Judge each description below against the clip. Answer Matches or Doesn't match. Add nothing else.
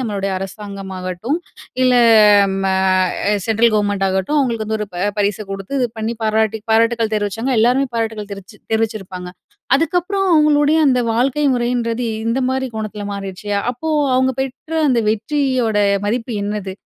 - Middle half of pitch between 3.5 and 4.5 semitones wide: Matches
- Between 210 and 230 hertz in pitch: Matches